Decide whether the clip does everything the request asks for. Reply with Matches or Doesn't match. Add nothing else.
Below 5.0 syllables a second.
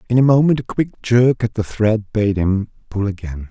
Doesn't match